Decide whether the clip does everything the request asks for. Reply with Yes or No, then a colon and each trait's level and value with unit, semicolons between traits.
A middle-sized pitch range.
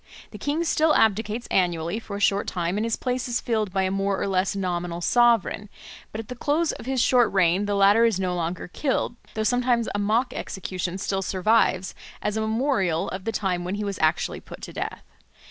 Yes: average, 3.8 semitones